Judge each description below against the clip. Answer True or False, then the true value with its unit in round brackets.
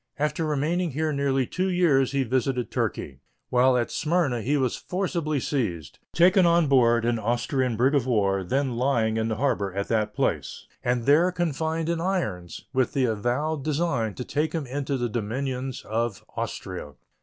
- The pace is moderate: True (170 wpm)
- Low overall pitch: True (130 Hz)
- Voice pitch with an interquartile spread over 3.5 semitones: True (4.7 semitones)